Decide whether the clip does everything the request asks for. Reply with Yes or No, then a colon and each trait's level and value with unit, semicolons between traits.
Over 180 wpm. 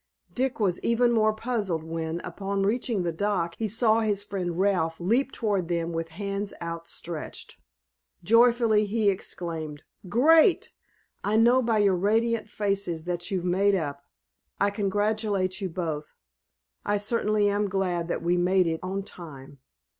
No: average, 145 wpm